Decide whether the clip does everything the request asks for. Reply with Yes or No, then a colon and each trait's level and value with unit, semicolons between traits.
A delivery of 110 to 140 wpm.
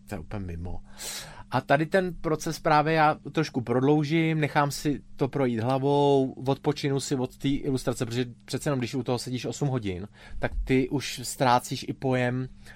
No: average, 165 wpm